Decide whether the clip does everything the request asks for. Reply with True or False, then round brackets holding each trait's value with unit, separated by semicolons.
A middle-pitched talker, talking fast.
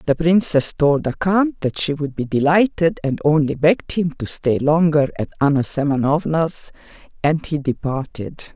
False (150 Hz; 160 wpm)